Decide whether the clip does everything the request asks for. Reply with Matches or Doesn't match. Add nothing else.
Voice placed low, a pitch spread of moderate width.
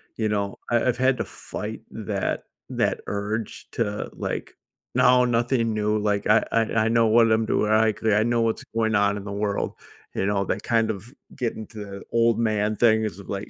Doesn't match